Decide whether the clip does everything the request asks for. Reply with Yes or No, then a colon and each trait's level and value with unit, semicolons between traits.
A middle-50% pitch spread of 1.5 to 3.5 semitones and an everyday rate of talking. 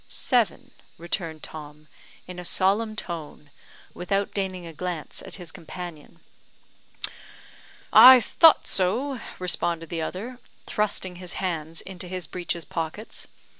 No: average, 3.2 semitones; slow, 120 wpm